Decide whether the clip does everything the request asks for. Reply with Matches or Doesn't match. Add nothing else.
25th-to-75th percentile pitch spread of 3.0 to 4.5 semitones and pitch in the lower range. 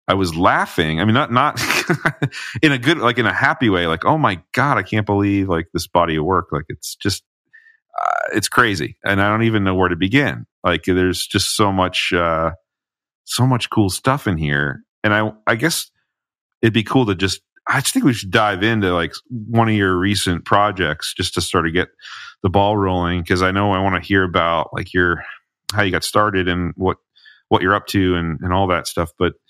Matches